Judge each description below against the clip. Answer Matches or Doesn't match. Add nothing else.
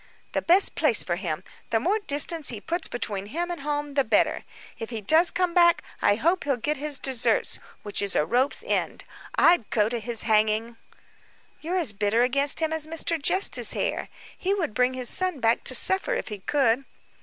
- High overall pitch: Matches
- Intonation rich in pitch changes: Matches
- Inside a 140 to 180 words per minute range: Doesn't match